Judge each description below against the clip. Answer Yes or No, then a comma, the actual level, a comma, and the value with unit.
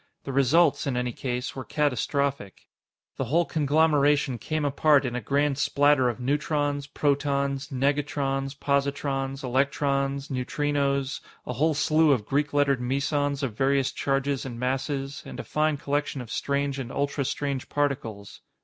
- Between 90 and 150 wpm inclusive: Yes, average, 140 wpm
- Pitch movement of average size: No, narrow, 1.4 semitones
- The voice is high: No, medium, 140 Hz